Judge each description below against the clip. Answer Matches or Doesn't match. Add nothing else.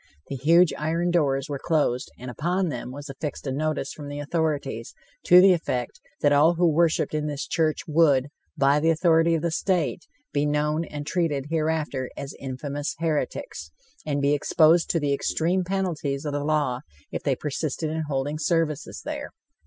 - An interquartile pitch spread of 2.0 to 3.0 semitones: Matches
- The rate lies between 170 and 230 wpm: Matches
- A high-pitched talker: Doesn't match